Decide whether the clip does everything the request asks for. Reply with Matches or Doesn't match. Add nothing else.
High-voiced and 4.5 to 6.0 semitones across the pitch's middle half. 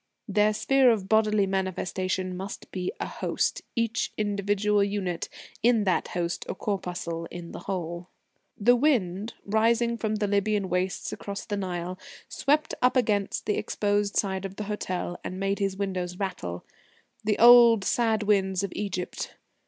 Doesn't match